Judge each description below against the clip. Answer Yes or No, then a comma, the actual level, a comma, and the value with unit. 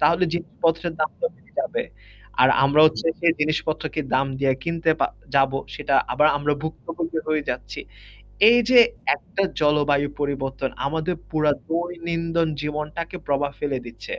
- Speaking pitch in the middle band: Yes, medium, 155 Hz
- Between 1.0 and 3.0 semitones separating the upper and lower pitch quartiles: Yes, average, 2.7 semitones